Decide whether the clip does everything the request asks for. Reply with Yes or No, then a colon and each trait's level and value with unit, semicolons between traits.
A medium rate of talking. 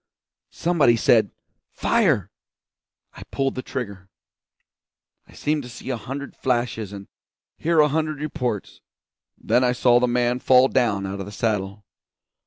Yes: average, 145 wpm